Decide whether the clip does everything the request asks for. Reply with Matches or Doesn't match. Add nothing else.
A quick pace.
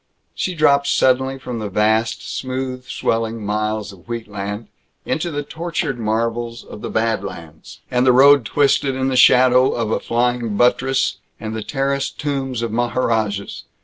Doesn't match